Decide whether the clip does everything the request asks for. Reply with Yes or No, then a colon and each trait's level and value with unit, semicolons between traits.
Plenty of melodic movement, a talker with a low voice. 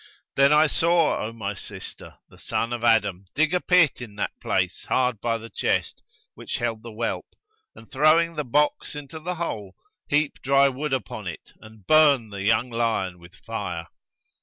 Yes: wide, 5.7 semitones; low, 120 Hz